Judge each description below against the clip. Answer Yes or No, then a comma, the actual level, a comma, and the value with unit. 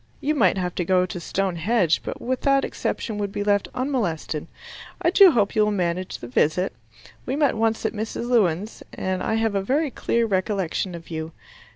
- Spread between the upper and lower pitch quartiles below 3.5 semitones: No, average, 4.5 semitones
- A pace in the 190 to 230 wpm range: Yes, average, 200 wpm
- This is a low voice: No, high, 205 Hz